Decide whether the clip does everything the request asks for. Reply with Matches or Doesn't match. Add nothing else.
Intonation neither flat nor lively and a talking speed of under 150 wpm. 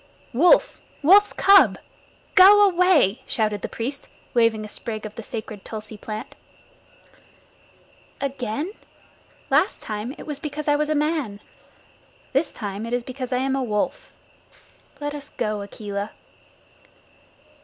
Doesn't match